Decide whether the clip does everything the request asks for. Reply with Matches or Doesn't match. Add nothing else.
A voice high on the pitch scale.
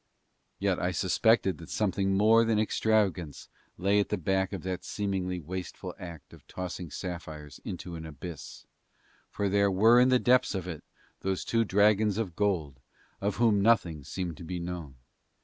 Doesn't match